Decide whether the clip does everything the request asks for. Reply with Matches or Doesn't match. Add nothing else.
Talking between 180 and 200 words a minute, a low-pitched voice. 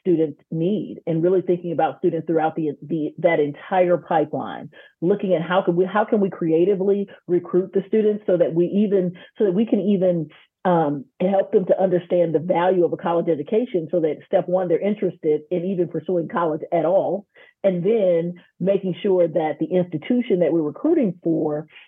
Doesn't match